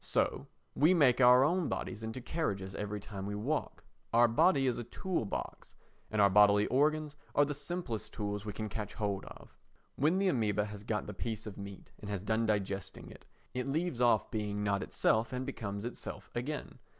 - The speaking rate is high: No, average, 190 wpm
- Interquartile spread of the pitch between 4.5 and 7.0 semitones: Yes, average, 5.0 semitones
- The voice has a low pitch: Yes, low, 110 Hz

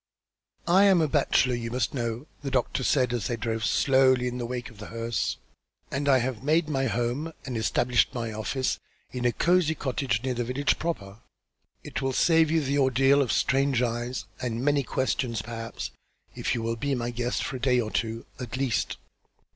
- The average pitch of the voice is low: Yes, low, 125 Hz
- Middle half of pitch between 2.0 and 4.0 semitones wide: Yes, average, 2.8 semitones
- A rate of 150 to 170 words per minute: No, average, 195 wpm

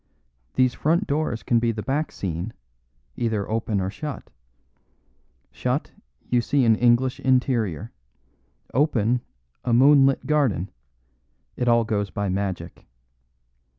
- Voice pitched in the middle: No, low, 120 Hz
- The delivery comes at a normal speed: No, slow, 115 wpm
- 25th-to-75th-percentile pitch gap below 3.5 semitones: No, average, 4.5 semitones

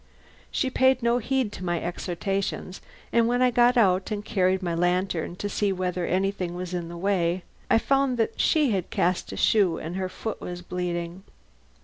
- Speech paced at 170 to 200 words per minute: Yes, average, 190 wpm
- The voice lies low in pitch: No, high, 190 Hz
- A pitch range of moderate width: Yes, average, 4.3 semitones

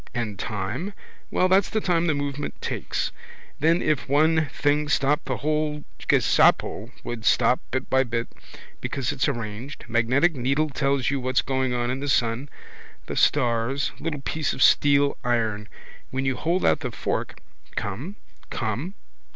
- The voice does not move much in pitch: No, average, 3.9 semitones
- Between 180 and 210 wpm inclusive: No, average, 160 wpm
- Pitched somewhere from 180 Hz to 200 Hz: No, low, 135 Hz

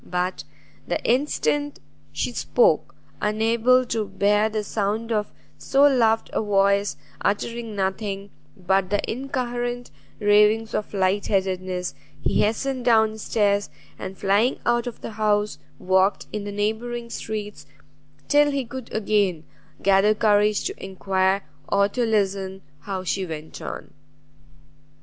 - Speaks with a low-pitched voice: No, high, 210 Hz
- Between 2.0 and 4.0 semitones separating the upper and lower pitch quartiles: Yes, average, 2.9 semitones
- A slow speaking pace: Yes, slow, 125 wpm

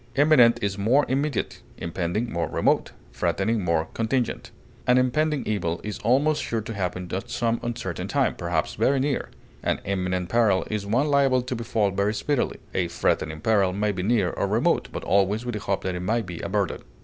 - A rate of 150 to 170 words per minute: No, average, 185 wpm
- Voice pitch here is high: No, low, 110 Hz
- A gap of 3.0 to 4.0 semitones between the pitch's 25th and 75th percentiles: No, average, 5.0 semitones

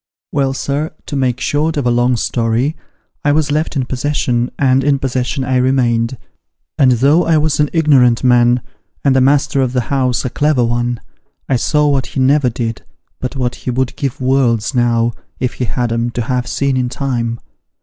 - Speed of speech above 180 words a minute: Yes, average, 200 wpm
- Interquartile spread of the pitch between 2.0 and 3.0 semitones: Yes, narrow, 2.5 semitones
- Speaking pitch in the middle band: No, low, 130 Hz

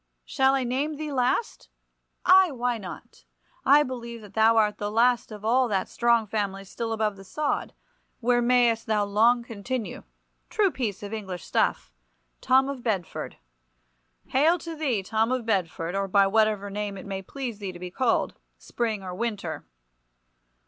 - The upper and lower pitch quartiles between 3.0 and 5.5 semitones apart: Yes, average, 4.1 semitones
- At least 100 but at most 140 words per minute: No, average, 160 wpm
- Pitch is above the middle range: Yes, high, 225 Hz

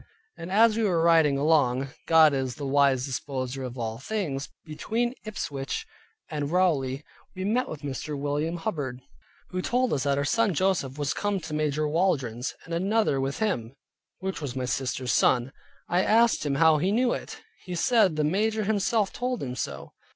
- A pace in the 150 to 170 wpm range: No, average, 180 wpm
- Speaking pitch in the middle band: Yes, medium, 155 Hz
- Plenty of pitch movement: Yes, wide, 6.1 semitones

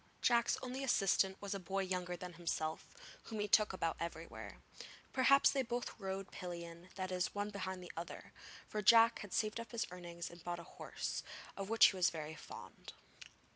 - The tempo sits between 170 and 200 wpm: Yes, average, 185 wpm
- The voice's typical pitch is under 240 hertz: Yes, high, 190 Hz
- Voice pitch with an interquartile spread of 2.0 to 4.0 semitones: Yes, average, 3.6 semitones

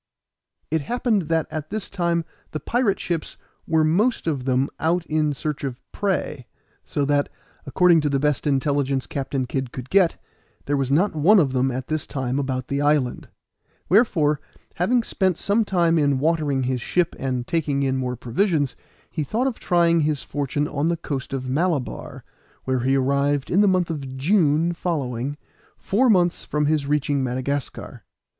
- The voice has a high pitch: No, medium, 150 Hz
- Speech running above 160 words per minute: Yes, average, 170 wpm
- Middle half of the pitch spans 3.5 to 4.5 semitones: Yes, average, 4.2 semitones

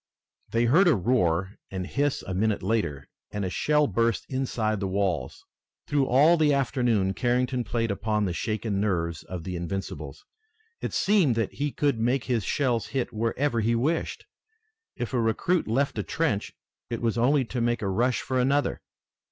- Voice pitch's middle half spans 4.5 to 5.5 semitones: Yes, average, 5.0 semitones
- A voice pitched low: Yes, low, 115 Hz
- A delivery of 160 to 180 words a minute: Yes, average, 175 wpm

